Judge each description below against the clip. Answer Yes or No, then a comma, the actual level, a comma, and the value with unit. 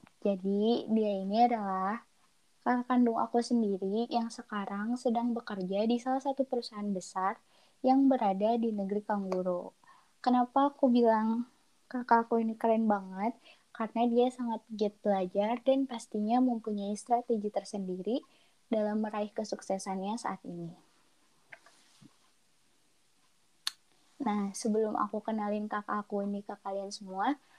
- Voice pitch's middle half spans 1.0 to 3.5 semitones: Yes, average, 2.9 semitones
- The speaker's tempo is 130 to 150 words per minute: No, average, 115 wpm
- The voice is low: No, high, 220 Hz